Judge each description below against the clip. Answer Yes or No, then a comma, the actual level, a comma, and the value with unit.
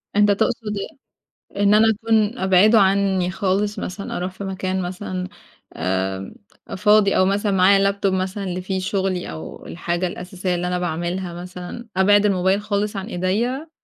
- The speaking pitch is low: No, high, 190 Hz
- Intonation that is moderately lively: No, narrow, 2.1 semitones